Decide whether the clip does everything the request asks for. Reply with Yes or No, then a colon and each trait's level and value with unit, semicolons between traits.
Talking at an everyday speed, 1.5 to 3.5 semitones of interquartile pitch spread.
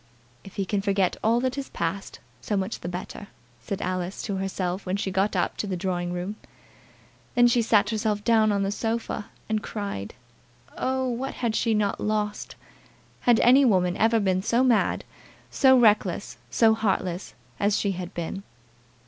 Yes: average, 175 wpm; average, 3.1 semitones